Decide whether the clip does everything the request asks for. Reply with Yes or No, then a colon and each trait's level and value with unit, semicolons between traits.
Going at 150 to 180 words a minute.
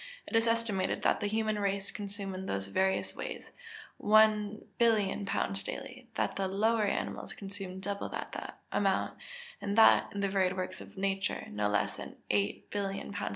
Yes: average, 160 wpm